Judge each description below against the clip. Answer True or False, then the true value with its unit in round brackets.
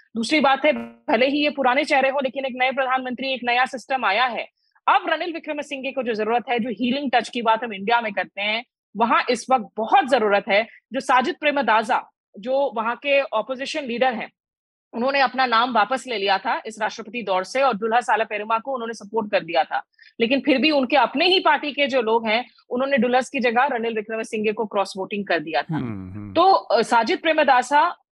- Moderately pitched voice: False (245 Hz)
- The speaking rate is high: True (215 wpm)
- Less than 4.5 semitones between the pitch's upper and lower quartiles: True (3.4 semitones)